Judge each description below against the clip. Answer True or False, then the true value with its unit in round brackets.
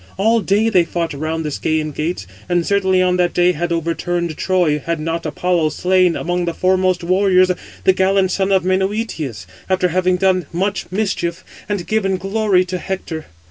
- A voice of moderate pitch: True (180 Hz)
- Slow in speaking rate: False (175 wpm)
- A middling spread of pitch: False (2.2 semitones)